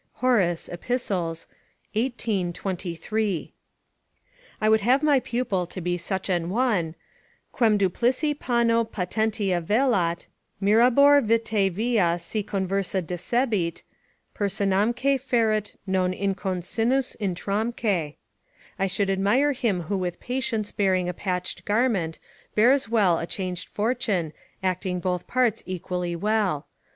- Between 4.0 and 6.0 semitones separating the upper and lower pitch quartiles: Yes, average, 4.3 semitones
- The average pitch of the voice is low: No, high, 200 Hz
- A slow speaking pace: Yes, slow, 115 wpm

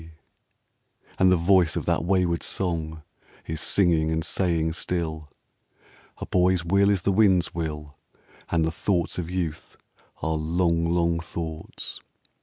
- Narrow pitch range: Yes, narrow, 2.2 semitones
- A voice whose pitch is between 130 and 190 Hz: No, very low, 85 Hz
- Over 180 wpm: No, average, 145 wpm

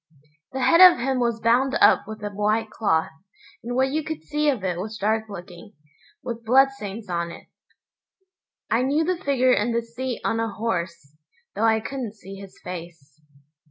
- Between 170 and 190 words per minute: Yes, average, 180 wpm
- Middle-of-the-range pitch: No, high, 225 Hz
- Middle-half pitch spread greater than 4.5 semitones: Yes, average, 4.9 semitones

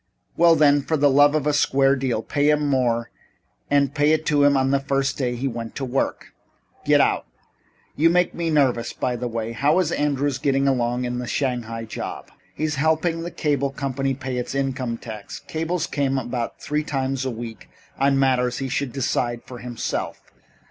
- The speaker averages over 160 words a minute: Yes, average, 190 wpm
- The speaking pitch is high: No, low, 135 Hz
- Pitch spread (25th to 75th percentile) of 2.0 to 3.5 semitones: Yes, average, 2.9 semitones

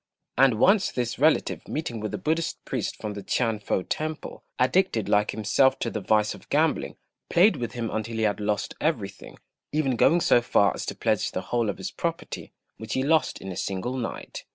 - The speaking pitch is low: Yes, low, 120 Hz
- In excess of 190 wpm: Yes, average, 200 wpm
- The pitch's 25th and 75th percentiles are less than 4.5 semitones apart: No, wide, 5.6 semitones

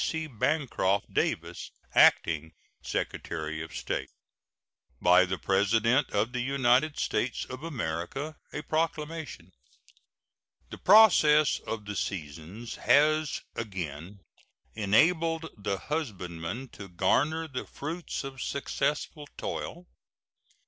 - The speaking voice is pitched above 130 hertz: No, low, 125 Hz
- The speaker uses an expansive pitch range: Yes, wide, 8.3 semitones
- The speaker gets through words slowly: Yes, slow, 100 wpm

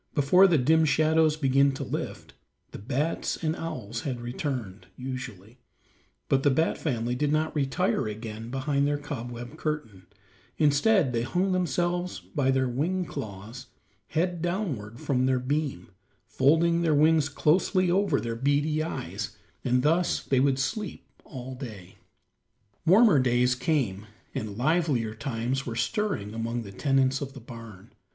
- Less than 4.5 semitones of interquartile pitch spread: No, average, 4.8 semitones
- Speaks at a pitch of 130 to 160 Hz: Yes, low, 135 Hz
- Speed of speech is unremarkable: Yes, average, 145 wpm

